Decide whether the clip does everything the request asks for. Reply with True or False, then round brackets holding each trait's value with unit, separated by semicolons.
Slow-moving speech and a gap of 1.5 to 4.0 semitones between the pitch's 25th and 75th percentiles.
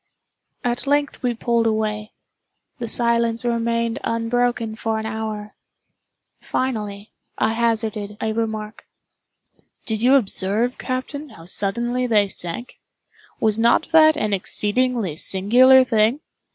True (115 wpm; 2.4 semitones)